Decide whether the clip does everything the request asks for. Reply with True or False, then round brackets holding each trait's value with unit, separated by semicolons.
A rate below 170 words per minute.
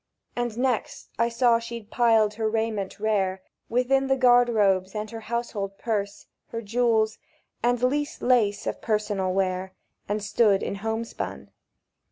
True (145 wpm)